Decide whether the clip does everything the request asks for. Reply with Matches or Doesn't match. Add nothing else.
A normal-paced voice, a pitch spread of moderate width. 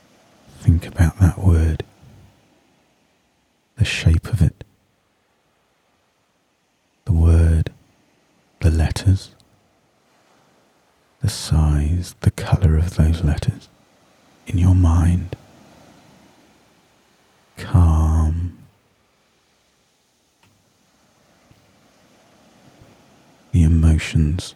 Doesn't match